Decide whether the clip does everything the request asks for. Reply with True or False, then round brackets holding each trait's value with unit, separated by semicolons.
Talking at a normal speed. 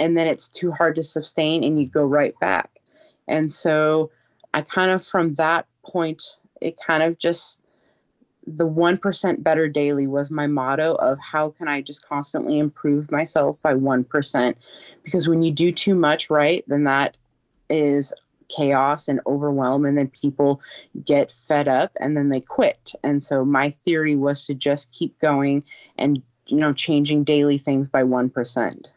True (170 wpm)